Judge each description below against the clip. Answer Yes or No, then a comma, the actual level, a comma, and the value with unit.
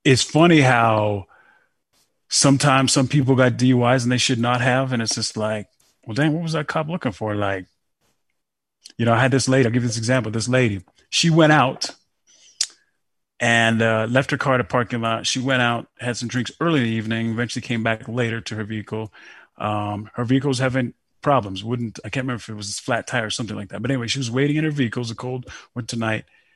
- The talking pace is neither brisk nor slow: No, fast, 225 wpm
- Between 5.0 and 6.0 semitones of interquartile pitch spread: No, average, 2.9 semitones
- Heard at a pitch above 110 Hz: Yes, low, 125 Hz